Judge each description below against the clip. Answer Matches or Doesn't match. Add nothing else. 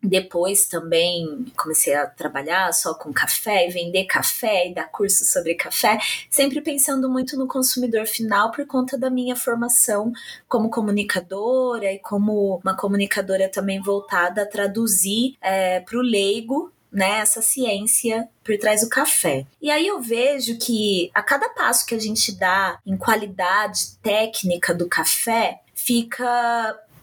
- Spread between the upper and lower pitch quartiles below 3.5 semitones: Doesn't match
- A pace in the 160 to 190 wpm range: Doesn't match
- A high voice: Matches